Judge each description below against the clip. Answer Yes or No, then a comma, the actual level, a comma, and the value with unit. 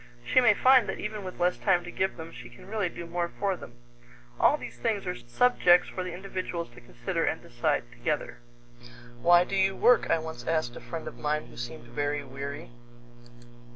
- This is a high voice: No, medium, 170 Hz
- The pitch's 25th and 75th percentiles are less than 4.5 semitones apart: No, average, 5.3 semitones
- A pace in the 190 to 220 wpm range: Yes, average, 200 wpm